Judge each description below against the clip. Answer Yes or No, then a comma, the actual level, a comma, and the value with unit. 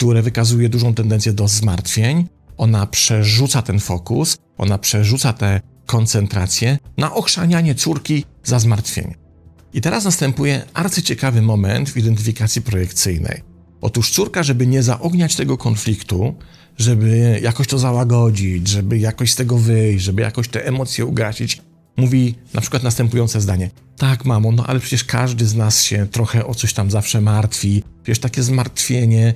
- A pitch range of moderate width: Yes, average, 3.2 semitones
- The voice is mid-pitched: No, low, 115 Hz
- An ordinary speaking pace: Yes, average, 145 wpm